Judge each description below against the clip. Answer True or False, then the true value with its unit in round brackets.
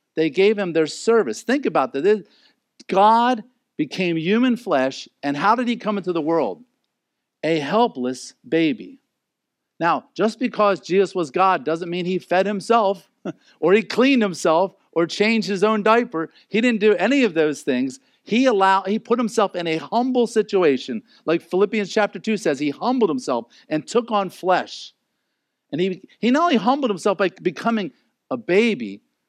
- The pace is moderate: True (170 wpm)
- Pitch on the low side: False (205 Hz)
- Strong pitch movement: False (4.7 semitones)